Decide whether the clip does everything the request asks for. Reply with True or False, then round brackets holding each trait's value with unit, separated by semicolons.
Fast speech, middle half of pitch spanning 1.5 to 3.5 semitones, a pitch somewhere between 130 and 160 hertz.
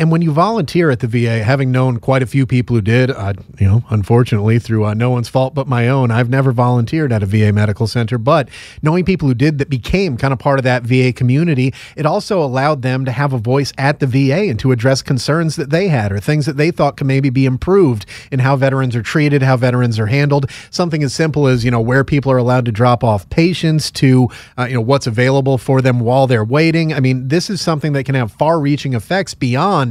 True (245 wpm; 3.2 semitones; 135 Hz)